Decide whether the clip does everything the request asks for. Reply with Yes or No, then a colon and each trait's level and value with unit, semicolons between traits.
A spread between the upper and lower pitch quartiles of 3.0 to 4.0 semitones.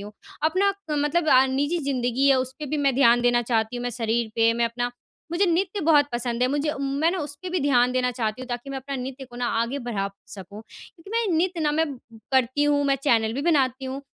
Yes: average, 3.5 semitones